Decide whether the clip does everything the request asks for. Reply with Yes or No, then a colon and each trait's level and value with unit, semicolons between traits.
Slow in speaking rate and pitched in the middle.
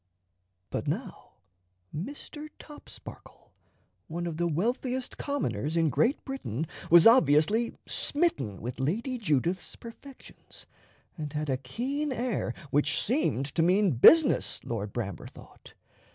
Yes: slow, 120 wpm; medium, 175 Hz